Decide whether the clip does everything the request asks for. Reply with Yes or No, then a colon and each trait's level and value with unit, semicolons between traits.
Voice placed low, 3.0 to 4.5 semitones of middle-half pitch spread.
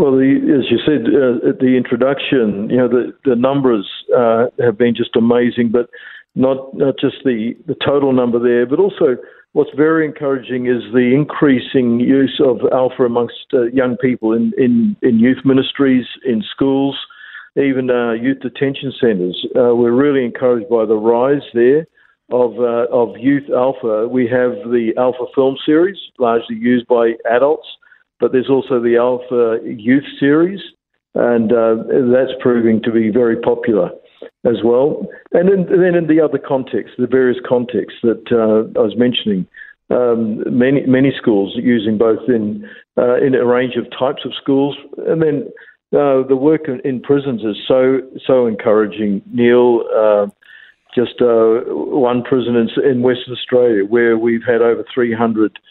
No: low, 125 Hz; narrow, 2.5 semitones